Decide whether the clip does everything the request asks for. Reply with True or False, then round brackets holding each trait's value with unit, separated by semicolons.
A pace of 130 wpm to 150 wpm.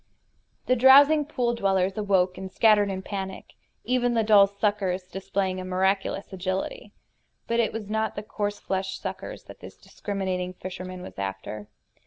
False (160 wpm)